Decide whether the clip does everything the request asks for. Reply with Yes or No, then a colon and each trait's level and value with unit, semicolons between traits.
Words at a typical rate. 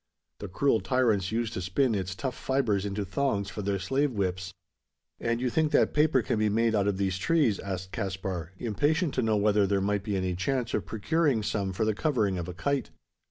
No: fast, 210 wpm